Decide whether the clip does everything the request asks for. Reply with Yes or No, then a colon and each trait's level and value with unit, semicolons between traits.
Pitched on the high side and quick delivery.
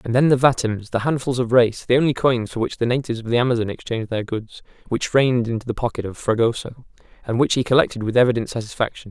No: low, 120 Hz; fast, 215 wpm